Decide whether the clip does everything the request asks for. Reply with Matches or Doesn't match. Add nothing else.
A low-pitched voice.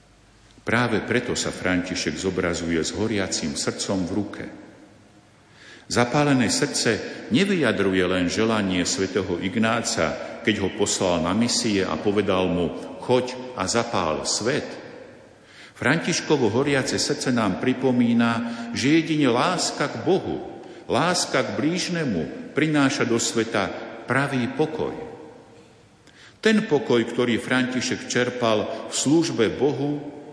Matches